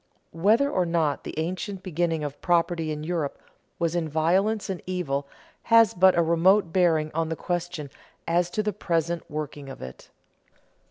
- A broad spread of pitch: No, average, 2.8 semitones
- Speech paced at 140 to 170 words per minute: Yes, average, 165 wpm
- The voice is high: No, medium, 170 Hz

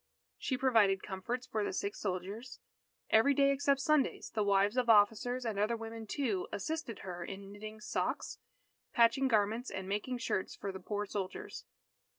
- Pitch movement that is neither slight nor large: Yes, average, 3.9 semitones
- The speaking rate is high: No, average, 165 wpm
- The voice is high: Yes, high, 220 Hz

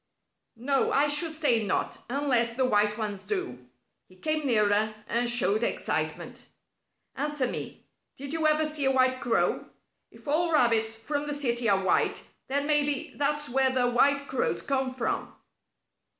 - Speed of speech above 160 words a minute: No, average, 155 wpm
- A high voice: Yes, very high, 260 Hz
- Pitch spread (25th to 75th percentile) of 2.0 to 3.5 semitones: No, average, 4.3 semitones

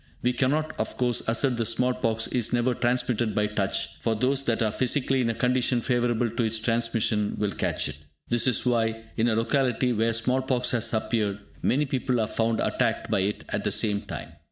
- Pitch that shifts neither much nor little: No, narrow, 2.0 semitones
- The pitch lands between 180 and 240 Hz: No, low, 120 Hz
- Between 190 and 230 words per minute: Yes, fast, 205 wpm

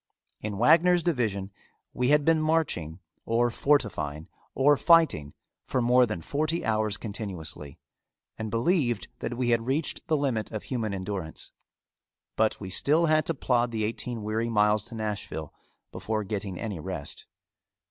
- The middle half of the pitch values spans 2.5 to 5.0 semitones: No, wide, 5.4 semitones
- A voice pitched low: Yes, low, 115 Hz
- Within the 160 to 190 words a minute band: No, average, 145 wpm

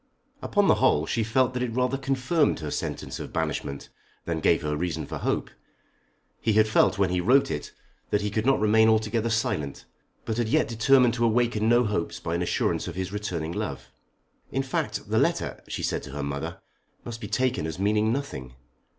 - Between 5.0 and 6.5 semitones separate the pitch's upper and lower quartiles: Yes, wide, 5.6 semitones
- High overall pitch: No, low, 110 Hz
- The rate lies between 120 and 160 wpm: No, average, 200 wpm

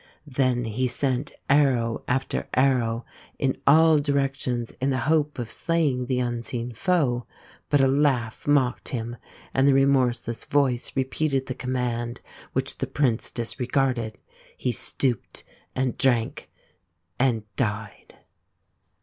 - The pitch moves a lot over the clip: No, narrow, 2.4 semitones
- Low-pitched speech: Yes, low, 130 Hz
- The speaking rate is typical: No, slow, 125 wpm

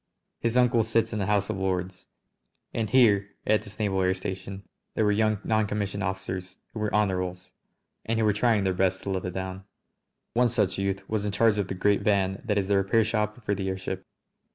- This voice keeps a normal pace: No, fast, 210 wpm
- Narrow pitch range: Yes, narrow, 2.3 semitones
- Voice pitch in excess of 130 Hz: No, low, 100 Hz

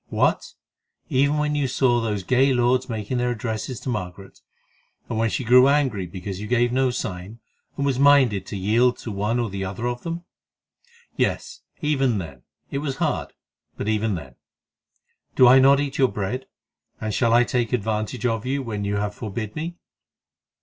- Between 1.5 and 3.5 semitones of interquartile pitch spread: No, average, 4.0 semitones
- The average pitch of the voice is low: Yes, low, 120 Hz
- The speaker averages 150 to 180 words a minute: Yes, average, 175 wpm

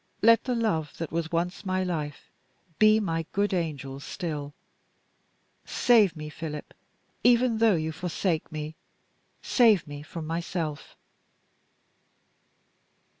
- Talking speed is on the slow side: Yes, slow, 115 wpm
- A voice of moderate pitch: Yes, medium, 170 Hz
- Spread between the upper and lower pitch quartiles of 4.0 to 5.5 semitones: Yes, average, 5.1 semitones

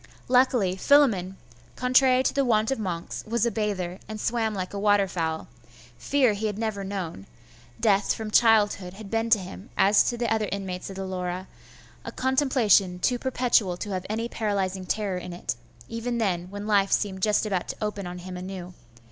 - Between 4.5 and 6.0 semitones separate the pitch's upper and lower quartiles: No, average, 3.5 semitones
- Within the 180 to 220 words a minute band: Yes, average, 190 wpm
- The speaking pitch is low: No, high, 205 Hz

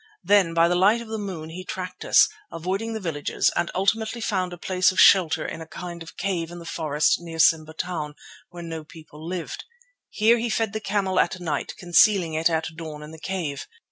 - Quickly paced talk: Yes, fast, 215 wpm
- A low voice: No, medium, 175 Hz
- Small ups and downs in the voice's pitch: No, average, 3.3 semitones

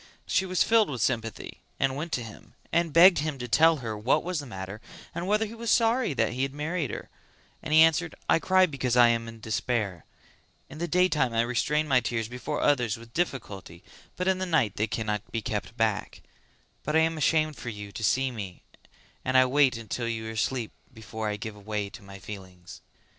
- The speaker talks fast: Yes, fast, 210 wpm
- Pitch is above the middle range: No, low, 125 Hz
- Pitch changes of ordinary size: No, wide, 6.2 semitones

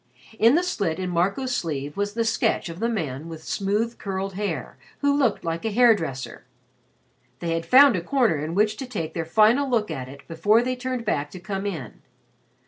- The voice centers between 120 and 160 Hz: No, high, 200 Hz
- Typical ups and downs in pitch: No, wide, 6.0 semitones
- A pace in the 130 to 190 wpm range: No, fast, 205 wpm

